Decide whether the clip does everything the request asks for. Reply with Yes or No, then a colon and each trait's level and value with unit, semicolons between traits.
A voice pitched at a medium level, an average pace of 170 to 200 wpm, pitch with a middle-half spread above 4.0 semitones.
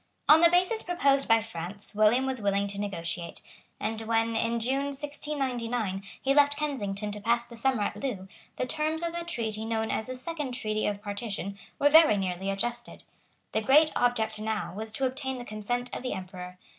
No: high, 230 Hz; average, 190 wpm; average, 4.7 semitones